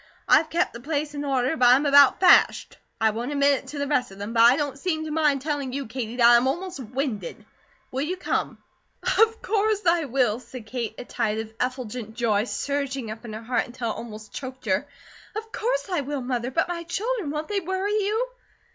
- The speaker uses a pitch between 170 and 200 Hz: No, very high, 275 Hz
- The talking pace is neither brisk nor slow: No, fast, 220 wpm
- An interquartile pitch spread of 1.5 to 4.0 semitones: No, average, 5.1 semitones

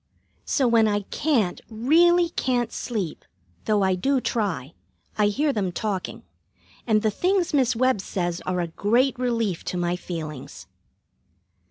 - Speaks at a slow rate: No, average, 145 wpm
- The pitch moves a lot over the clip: Yes, wide, 5.8 semitones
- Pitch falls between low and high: No, high, 220 Hz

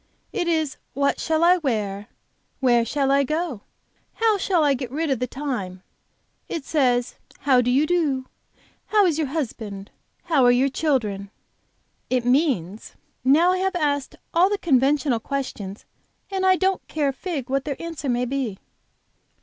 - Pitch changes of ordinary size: Yes, average, 4.8 semitones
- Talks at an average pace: Yes, average, 165 wpm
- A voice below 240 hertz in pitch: No, very high, 275 Hz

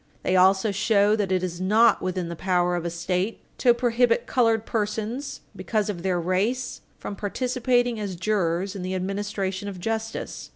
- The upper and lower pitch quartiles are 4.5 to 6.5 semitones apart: No, average, 3.4 semitones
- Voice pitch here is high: Yes, high, 200 Hz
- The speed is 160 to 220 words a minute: Yes, average, 170 wpm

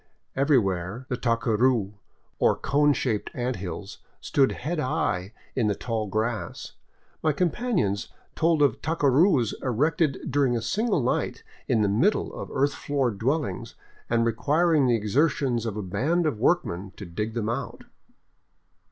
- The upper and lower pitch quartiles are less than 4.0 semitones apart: No, wide, 5.4 semitones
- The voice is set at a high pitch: No, low, 125 Hz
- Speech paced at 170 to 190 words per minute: No, average, 145 wpm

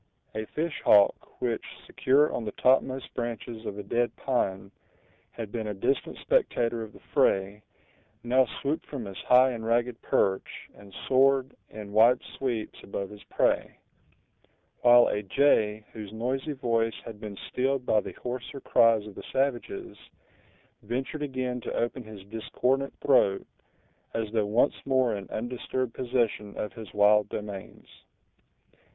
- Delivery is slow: No, average, 145 wpm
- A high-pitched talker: No, low, 115 Hz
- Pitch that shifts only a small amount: No, average, 3.5 semitones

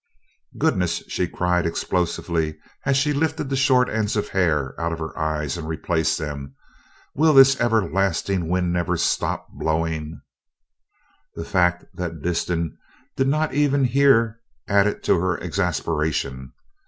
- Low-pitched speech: Yes, very low, 90 Hz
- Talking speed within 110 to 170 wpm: Yes, slow, 135 wpm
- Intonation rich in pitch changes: Yes, wide, 6.1 semitones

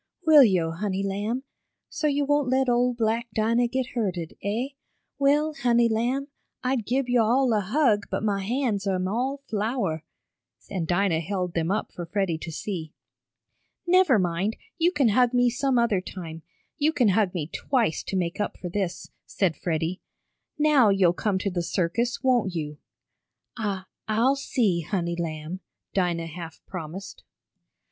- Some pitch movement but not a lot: No, wide, 5.7 semitones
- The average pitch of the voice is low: No, high, 210 Hz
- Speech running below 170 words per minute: Yes, average, 160 wpm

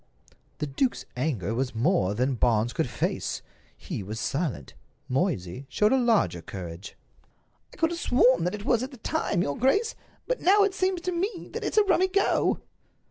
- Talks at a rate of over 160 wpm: Yes, average, 185 wpm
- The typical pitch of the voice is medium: Yes, medium, 180 Hz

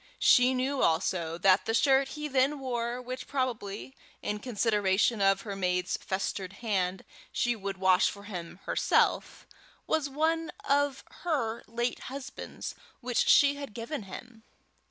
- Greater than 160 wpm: No, average, 140 wpm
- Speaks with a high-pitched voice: Yes, high, 235 Hz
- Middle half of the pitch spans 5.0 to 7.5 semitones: Yes, wide, 5.5 semitones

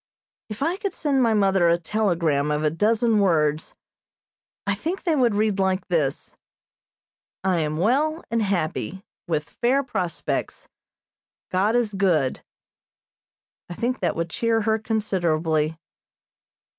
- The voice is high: Yes, high, 195 Hz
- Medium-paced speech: No, slow, 130 wpm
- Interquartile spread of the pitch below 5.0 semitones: No, wide, 5.6 semitones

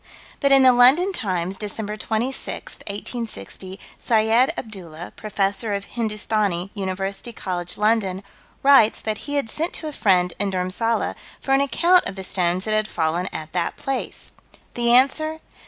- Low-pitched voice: No, high, 215 Hz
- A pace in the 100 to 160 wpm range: Yes, average, 155 wpm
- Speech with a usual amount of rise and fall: Yes, average, 4.7 semitones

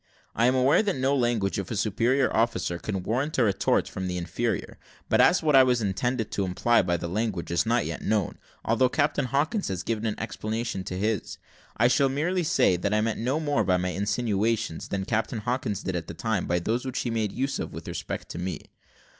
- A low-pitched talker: Yes, low, 115 Hz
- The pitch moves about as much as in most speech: Yes, average, 4.8 semitones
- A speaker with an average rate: No, fast, 220 wpm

